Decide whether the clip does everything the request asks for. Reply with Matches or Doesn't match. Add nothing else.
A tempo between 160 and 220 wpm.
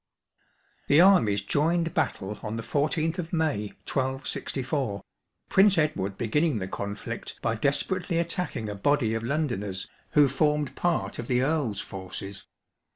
Doesn't match